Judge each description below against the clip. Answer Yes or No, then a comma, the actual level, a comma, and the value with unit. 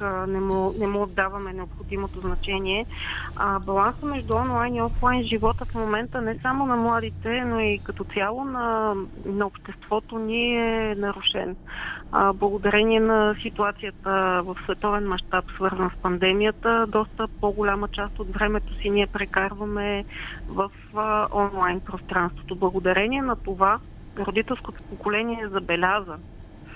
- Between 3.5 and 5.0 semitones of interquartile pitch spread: No, narrow, 2.5 semitones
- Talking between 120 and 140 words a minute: Yes, average, 130 wpm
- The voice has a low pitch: No, high, 205 Hz